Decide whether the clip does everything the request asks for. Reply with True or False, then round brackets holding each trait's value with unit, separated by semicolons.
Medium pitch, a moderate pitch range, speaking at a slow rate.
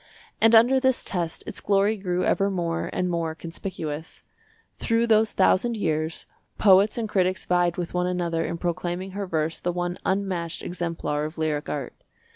False (180 Hz; 3.0 semitones; 165 wpm)